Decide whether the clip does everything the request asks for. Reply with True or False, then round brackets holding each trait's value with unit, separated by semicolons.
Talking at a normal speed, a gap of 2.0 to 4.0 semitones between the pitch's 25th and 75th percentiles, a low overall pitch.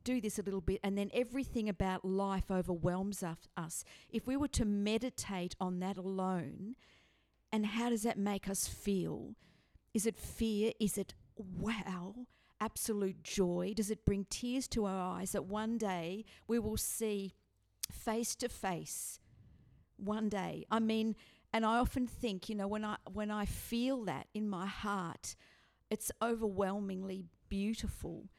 False (155 wpm; 2.8 semitones; 205 Hz)